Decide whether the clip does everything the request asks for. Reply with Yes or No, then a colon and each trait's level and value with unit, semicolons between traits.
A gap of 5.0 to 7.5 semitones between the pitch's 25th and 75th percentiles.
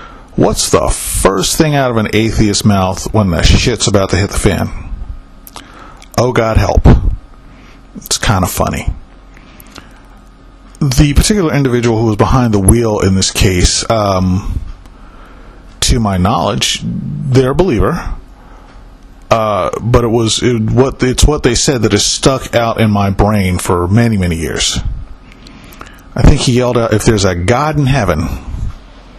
No: average, 4.5 semitones